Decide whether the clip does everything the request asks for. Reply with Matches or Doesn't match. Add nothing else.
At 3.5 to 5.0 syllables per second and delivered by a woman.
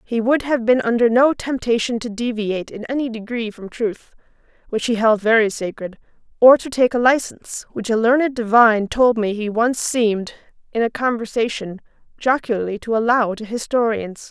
Doesn't match